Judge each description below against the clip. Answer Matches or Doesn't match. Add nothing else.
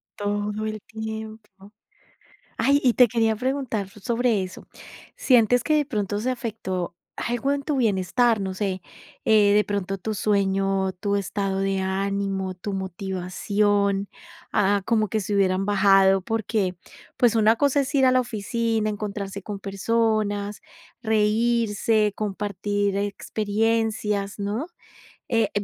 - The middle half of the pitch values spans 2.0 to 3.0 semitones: Matches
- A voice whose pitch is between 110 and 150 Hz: Doesn't match